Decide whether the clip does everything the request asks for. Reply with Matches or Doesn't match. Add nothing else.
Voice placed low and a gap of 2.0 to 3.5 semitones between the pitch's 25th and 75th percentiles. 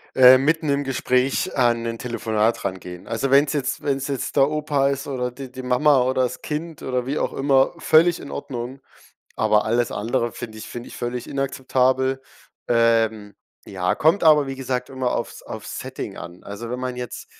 Matches